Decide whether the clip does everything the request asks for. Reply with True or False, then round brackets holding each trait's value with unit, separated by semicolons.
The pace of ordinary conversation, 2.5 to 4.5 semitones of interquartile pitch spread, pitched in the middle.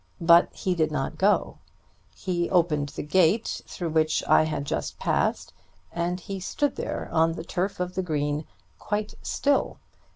True (160 wpm; 3.2 semitones; 175 Hz)